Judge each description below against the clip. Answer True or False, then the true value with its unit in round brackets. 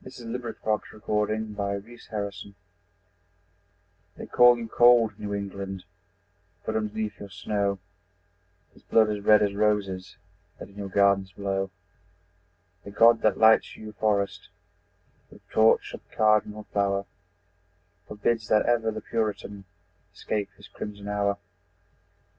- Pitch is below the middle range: True (105 Hz)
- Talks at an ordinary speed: False (125 wpm)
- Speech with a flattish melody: True (1.5 semitones)